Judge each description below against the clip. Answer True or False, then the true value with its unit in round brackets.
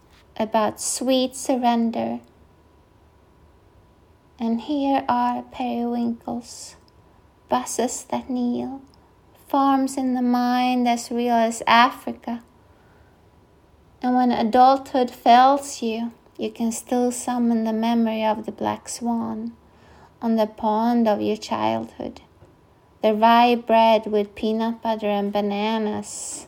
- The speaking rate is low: True (105 wpm)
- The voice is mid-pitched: False (225 Hz)